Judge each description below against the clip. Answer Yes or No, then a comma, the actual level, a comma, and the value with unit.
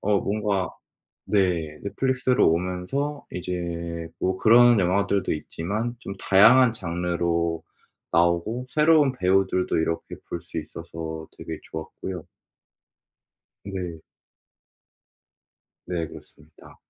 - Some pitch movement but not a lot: Yes, average, 4.3 semitones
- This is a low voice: Yes, very low, 90 Hz